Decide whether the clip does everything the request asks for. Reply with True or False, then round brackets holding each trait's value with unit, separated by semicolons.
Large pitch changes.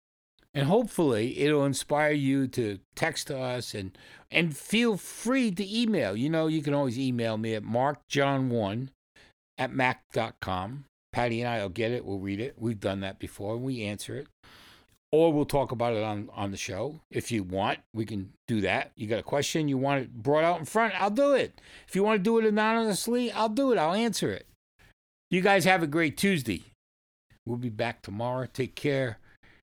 True (6.6 semitones)